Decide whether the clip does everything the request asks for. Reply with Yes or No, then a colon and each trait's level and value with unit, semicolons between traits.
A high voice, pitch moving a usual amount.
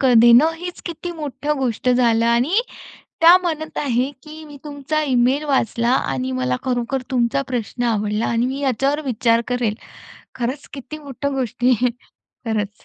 Yes: very high, 255 Hz; average, 3.7 semitones